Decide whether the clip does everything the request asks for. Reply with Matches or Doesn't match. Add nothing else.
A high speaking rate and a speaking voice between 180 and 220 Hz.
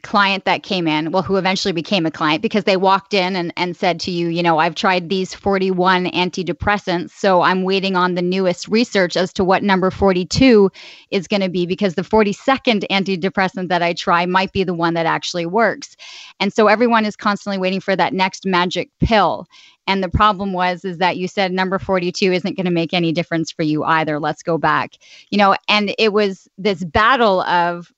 Matches